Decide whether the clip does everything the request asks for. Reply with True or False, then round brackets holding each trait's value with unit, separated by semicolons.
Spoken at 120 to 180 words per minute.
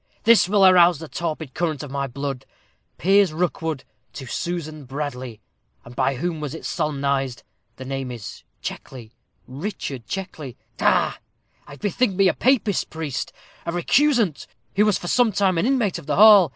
True (165 wpm)